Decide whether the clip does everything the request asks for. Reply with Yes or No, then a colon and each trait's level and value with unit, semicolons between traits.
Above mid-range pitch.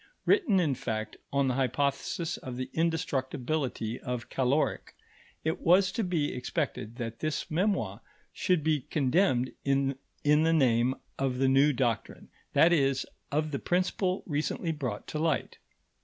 No: medium, 140 Hz